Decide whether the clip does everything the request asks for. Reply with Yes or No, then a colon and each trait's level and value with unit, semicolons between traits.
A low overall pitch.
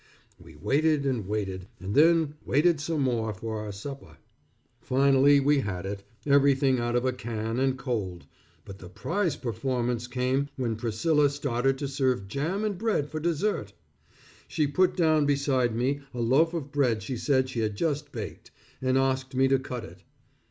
Yes: low, 130 Hz